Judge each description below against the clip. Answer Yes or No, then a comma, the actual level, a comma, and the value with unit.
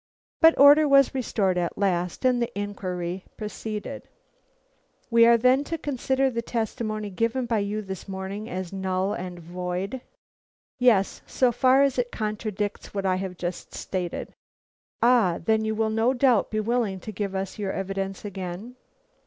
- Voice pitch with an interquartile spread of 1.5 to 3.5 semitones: No, average, 4.0 semitones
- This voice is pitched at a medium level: No, high, 210 Hz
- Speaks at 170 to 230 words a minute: No, average, 160 wpm